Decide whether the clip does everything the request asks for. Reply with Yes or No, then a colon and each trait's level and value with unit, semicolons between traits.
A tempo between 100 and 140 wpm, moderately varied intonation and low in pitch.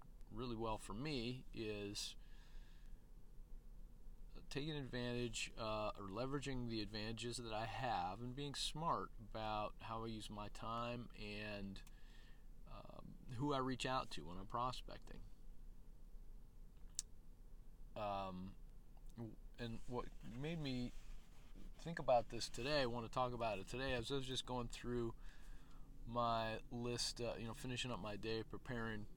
Yes: slow, 135 wpm; average, 3.1 semitones; low, 120 Hz